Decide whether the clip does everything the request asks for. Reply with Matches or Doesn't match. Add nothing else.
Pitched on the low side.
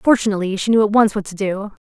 Doesn't match